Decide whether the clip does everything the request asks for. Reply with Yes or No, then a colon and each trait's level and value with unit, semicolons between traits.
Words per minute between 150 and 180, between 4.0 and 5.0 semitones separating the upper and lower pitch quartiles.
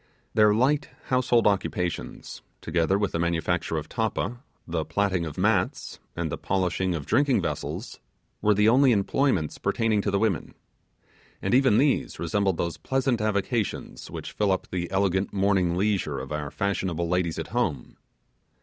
Yes: average, 155 wpm; average, 4.5 semitones